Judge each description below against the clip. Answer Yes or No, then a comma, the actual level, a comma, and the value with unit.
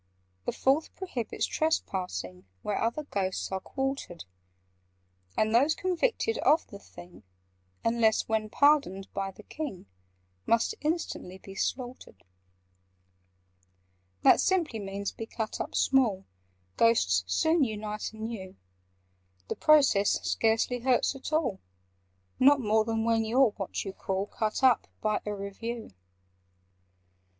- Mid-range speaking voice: No, high, 225 Hz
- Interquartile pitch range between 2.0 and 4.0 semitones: No, average, 5.3 semitones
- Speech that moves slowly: Yes, slow, 125 wpm